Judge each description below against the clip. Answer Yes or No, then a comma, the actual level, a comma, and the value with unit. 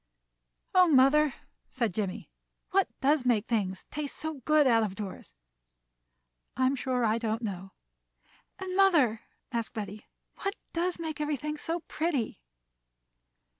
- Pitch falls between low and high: No, very high, 260 Hz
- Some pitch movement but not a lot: No, wide, 5.9 semitones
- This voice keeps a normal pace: No, slow, 130 wpm